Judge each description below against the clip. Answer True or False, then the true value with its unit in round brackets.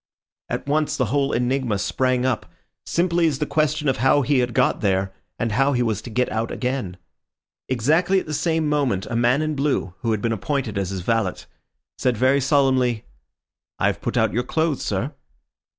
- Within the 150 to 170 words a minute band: False (195 wpm)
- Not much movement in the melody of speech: False (4.3 semitones)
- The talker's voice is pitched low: True (130 Hz)